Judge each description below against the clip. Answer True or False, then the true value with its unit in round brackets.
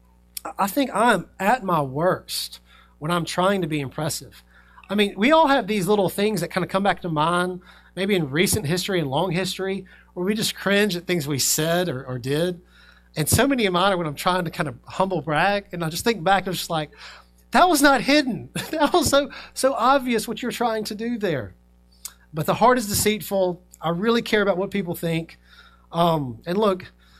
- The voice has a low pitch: False (180 Hz)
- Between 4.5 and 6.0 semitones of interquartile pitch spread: True (5.1 semitones)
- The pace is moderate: False (215 wpm)